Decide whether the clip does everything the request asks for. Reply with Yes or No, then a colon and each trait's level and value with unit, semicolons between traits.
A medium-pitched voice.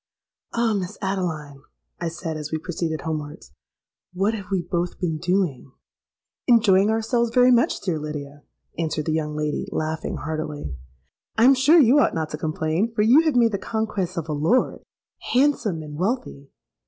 Yes: medium, 175 Hz